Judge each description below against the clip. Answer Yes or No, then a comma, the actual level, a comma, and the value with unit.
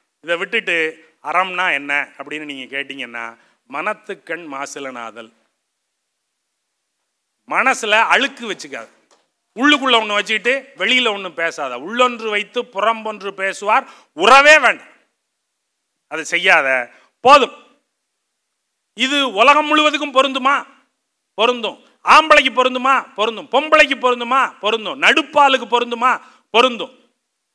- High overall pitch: Yes, high, 235 Hz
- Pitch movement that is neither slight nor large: No, wide, 6.3 semitones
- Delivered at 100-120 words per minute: No, average, 90 wpm